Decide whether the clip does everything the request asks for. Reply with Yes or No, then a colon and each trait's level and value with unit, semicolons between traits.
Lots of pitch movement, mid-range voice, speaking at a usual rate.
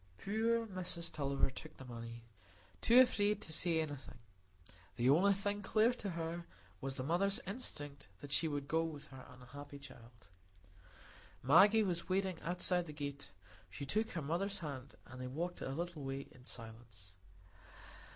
Yes: wide, 5.9 semitones; medium, 160 Hz; average, 160 wpm